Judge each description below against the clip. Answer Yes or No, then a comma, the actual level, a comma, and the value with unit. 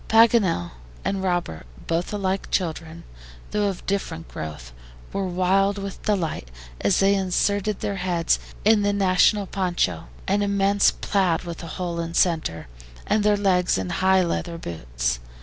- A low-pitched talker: No, medium, 185 Hz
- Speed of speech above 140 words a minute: Yes, average, 150 wpm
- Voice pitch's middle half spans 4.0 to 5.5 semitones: No, average, 3.2 semitones